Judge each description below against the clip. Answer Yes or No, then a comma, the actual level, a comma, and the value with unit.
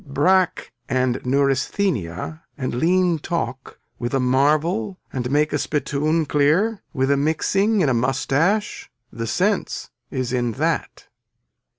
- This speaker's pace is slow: Yes, slow, 125 wpm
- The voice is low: No, medium, 145 Hz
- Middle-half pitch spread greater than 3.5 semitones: Yes, wide, 5.5 semitones